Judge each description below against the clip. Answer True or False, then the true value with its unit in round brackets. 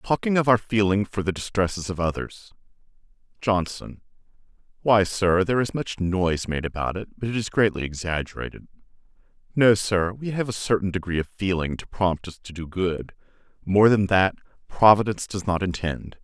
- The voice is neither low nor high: False (95 Hz)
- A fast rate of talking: False (165 wpm)